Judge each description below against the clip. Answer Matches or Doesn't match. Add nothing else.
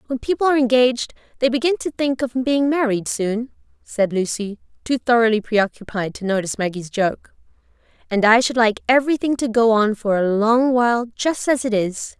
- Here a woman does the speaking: Matches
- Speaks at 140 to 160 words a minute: Doesn't match